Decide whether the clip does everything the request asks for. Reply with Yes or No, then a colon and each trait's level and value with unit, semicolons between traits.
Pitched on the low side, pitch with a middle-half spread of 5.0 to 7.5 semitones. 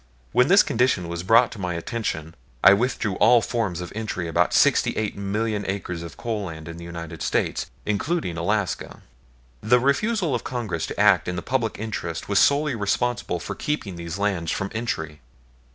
Yes: low, 100 Hz; wide, 5.5 semitones